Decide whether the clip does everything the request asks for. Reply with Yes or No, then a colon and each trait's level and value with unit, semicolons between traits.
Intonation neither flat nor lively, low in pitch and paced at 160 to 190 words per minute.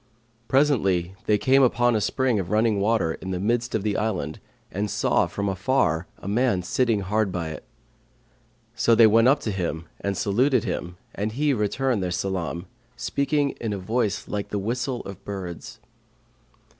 Yes: average, 4.3 semitones; low, 105 Hz; average, 170 wpm